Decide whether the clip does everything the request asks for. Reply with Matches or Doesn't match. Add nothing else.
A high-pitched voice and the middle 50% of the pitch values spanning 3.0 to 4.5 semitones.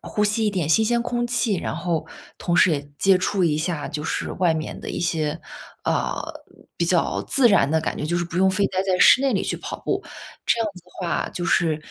Doesn't match